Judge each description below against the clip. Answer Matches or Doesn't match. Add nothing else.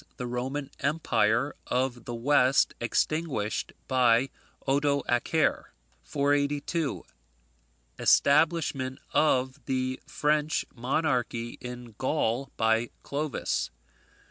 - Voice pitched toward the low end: Matches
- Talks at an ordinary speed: Doesn't match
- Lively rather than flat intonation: Doesn't match